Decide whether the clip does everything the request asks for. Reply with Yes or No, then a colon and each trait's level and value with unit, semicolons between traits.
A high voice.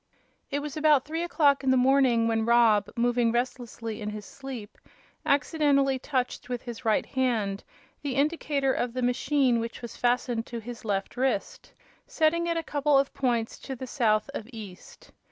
Yes: very high, 250 Hz